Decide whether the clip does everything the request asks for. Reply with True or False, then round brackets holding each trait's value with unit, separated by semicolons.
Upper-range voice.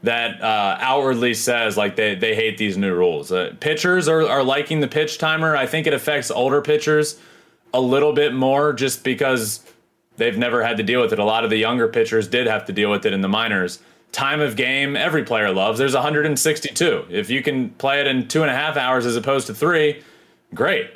False (140 Hz)